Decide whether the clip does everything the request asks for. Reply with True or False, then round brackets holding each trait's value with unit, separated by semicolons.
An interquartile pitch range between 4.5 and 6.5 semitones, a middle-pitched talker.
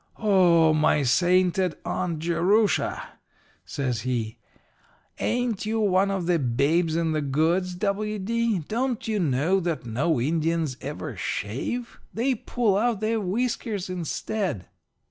True (5.6 semitones; 180 Hz)